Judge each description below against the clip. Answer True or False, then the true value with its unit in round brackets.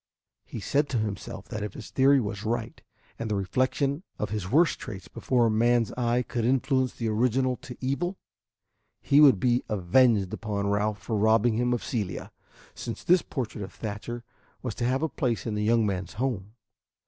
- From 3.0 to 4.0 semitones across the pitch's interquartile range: True (3.5 semitones)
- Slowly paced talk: False (185 wpm)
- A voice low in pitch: True (115 Hz)